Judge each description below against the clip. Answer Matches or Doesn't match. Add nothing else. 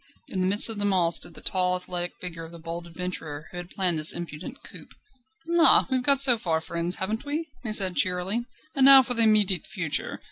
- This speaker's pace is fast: Matches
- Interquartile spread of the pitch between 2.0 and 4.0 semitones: Doesn't match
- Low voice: Doesn't match